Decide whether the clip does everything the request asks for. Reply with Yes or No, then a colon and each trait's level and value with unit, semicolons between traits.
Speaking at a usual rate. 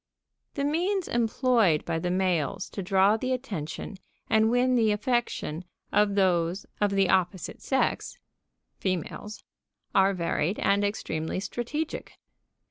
No: slow, 125 wpm